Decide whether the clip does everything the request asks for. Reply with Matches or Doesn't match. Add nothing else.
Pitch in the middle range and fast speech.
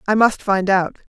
Doesn't match